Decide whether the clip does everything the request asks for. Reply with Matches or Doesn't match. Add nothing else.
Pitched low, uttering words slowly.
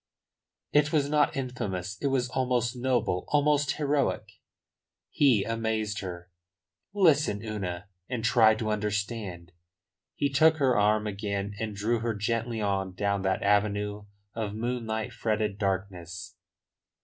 Matches